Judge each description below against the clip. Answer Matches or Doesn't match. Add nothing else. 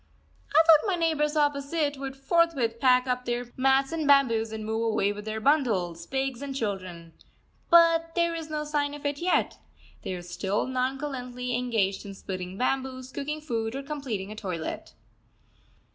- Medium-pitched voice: Doesn't match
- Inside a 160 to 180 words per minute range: Matches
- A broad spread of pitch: Doesn't match